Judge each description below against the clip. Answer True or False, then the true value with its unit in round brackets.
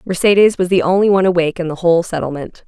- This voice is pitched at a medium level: True (175 Hz)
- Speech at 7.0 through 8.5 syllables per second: True (7.4 syllables/s)